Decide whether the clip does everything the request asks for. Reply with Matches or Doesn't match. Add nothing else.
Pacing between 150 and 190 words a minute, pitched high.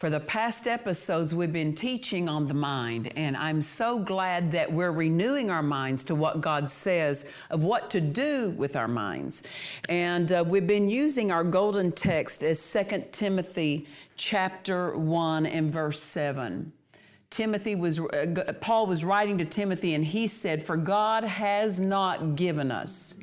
Doesn't match